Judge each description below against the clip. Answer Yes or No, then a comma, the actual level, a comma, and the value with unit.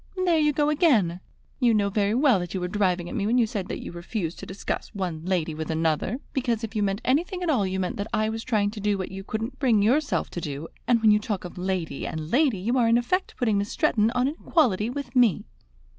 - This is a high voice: Yes, high, 210 Hz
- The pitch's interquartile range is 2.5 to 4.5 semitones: No, average, 5.0 semitones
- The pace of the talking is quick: Yes, fast, 255 wpm